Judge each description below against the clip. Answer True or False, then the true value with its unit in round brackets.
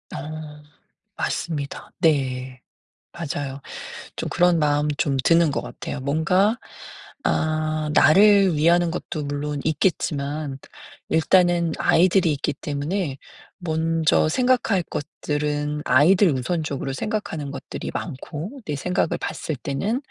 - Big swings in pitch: False (3.3 semitones)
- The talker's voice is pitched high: False (155 Hz)